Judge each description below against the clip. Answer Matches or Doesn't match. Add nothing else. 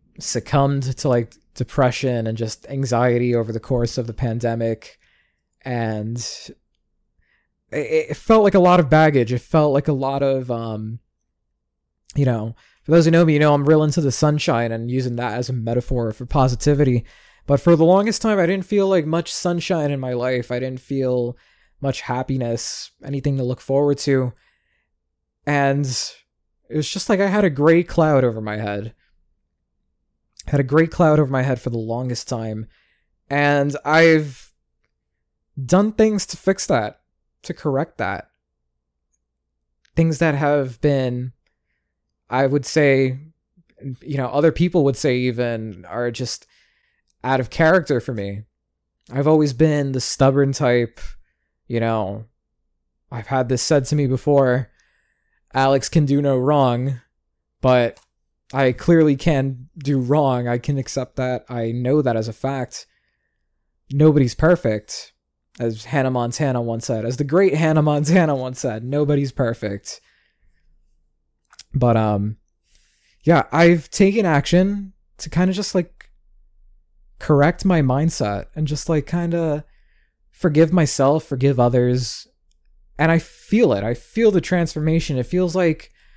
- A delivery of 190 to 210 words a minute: Doesn't match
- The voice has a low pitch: Matches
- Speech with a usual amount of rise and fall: Matches